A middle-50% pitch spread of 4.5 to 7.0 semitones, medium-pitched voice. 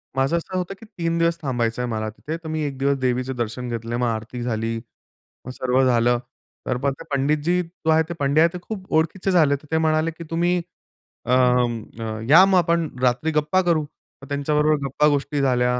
Yes: average, 5.0 semitones; medium, 145 Hz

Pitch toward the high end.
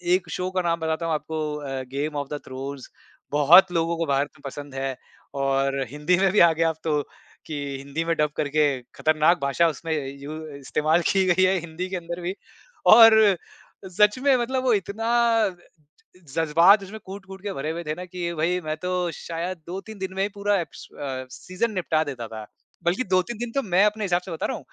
No: medium, 170 Hz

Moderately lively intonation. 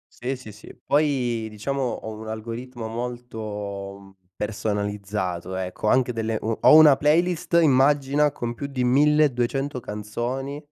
Yes: average, 4.5 semitones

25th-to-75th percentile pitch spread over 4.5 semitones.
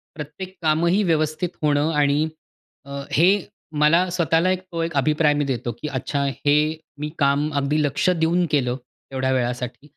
No: average, 2.9 semitones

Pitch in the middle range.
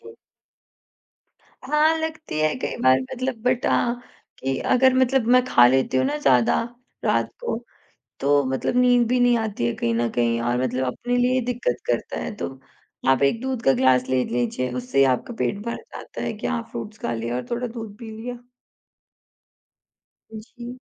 No: high, 215 Hz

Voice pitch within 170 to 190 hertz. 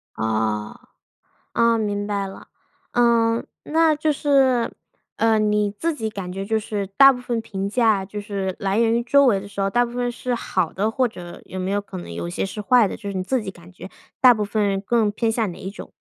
No: high, 210 Hz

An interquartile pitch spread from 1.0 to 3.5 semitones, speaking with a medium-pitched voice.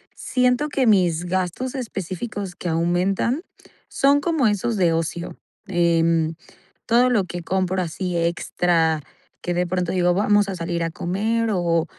No: average, 4.2 semitones; medium, 180 Hz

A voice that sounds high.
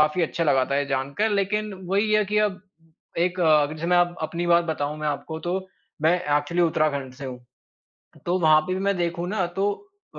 No: medium, 170 Hz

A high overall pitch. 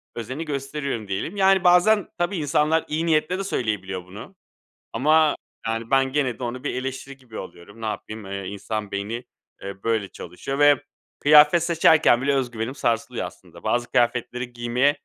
No: low, 130 Hz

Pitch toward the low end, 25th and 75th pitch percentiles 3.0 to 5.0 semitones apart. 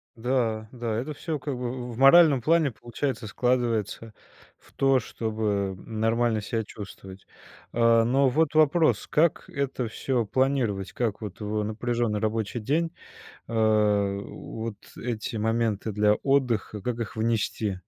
Yes: low, 115 Hz; average, 3.3 semitones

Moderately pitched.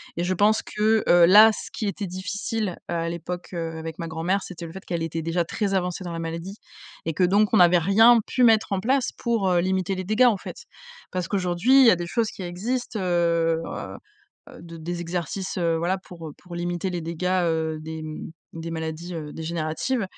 Yes: medium, 175 Hz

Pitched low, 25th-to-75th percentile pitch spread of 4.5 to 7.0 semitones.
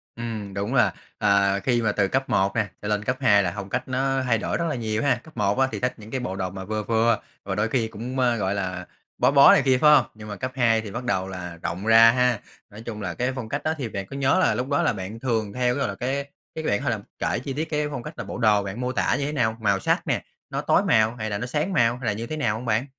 No: low, 115 Hz; average, 3.9 semitones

